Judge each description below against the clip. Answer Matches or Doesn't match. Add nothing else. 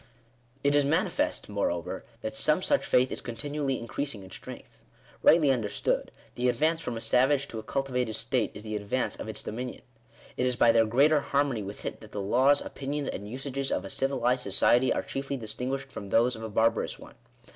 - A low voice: Matches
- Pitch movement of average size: Matches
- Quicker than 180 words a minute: Matches